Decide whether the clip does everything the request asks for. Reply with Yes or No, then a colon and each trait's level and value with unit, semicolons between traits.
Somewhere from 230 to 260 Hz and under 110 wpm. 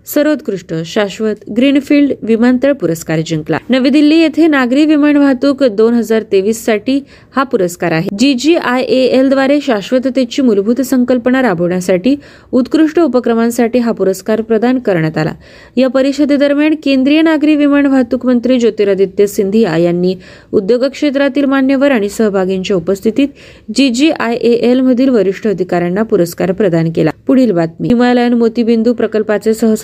No: high, 240 Hz; average, 115 wpm